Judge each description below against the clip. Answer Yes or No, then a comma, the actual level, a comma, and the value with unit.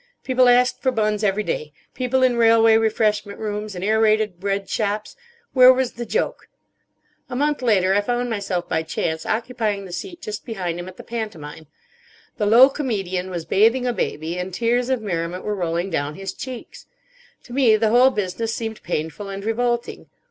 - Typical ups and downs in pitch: Yes, average, 4.4 semitones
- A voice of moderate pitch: No, high, 215 Hz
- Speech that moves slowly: No, average, 175 wpm